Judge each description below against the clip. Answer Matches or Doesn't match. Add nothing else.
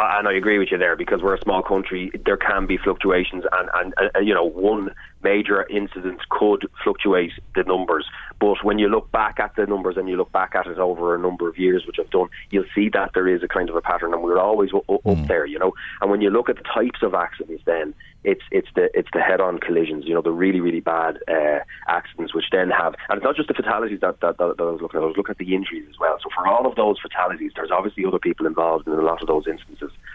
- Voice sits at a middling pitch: Doesn't match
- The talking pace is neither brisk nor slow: Doesn't match